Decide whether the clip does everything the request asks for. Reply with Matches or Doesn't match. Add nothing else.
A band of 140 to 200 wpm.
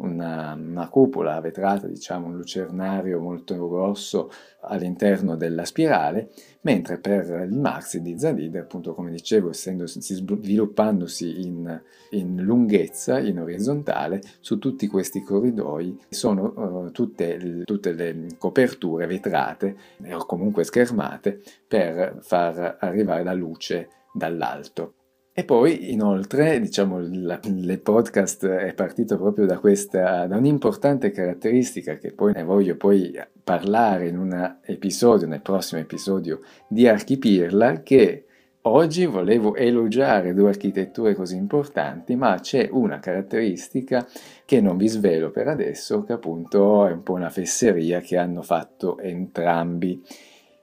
Doesn't match